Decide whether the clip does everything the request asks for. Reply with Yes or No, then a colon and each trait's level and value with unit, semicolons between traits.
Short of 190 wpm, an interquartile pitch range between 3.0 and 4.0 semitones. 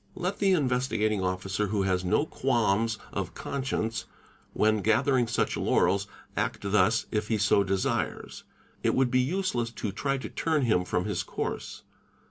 No: average, 160 wpm; average, 4.7 semitones